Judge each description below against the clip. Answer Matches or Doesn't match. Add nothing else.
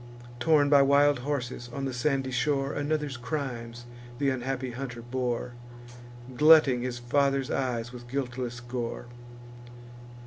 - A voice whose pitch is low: Matches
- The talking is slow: Matches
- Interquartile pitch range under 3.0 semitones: Matches